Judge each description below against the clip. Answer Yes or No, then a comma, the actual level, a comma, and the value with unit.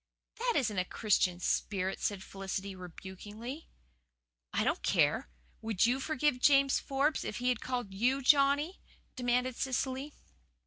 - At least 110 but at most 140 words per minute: Yes, slow, 135 wpm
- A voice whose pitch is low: No, very high, 250 Hz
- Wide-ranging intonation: Yes, wide, 5.7 semitones